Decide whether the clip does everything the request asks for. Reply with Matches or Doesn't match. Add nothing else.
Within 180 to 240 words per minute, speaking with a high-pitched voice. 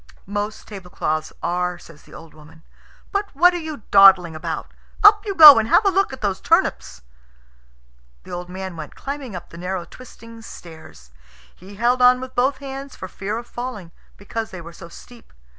Matches